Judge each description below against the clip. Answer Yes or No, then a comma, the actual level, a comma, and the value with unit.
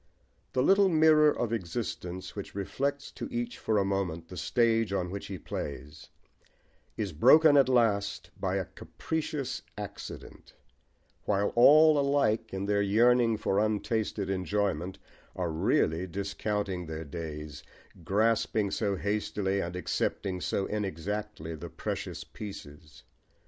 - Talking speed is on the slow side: Yes, slow, 130 wpm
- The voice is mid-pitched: No, low, 100 Hz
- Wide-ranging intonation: No, average, 4.2 semitones